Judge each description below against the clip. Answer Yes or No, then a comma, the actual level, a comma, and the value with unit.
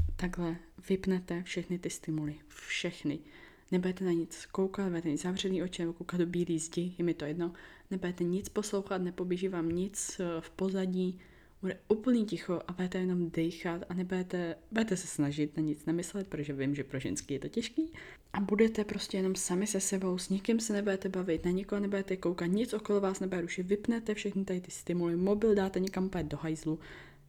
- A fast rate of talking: Yes, fast, 185 wpm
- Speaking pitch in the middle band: Yes, medium, 180 Hz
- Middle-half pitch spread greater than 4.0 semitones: No, narrow, 2.4 semitones